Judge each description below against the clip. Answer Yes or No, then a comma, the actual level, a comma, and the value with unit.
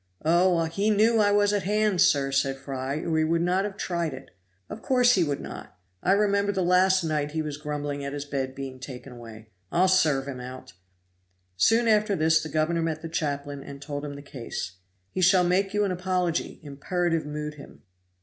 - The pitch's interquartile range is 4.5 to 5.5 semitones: Yes, average, 4.9 semitones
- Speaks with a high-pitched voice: No, medium, 160 Hz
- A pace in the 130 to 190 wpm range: No, average, 200 wpm